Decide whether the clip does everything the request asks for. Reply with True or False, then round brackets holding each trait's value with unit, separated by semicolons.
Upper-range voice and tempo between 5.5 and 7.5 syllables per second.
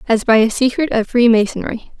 True (230 Hz; 5.6 syllables/s)